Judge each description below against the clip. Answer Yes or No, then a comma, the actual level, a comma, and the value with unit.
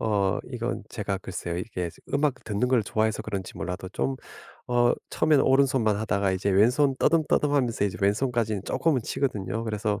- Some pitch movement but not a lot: Yes, average, 4.5 semitones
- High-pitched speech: No, low, 110 Hz